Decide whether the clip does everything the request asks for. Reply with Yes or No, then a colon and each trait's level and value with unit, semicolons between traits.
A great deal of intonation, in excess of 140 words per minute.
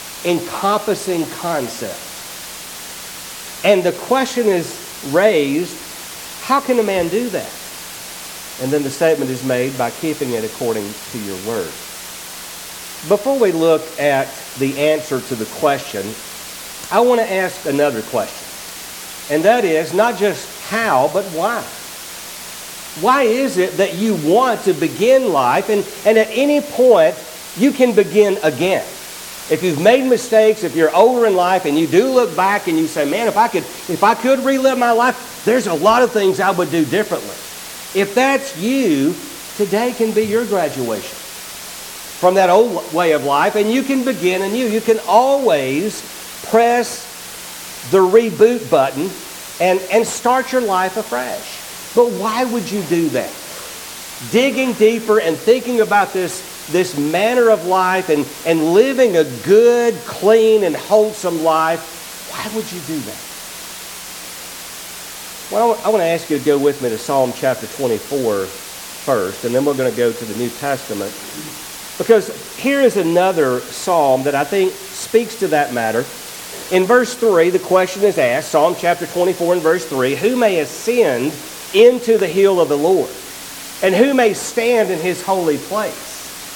Yes: wide, 6.6 semitones; average, 160 wpm